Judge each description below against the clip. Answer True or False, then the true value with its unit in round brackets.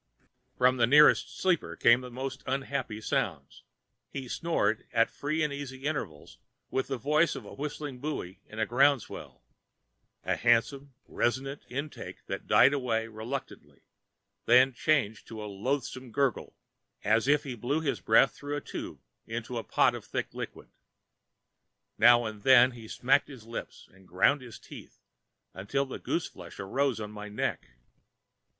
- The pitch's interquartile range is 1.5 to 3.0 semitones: False (3.8 semitones)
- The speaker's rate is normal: True (155 wpm)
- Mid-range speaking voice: False (130 Hz)